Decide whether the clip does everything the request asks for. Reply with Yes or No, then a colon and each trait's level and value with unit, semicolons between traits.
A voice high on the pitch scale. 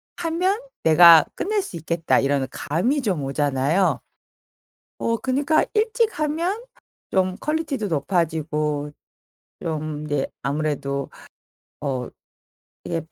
No: medium, 170 Hz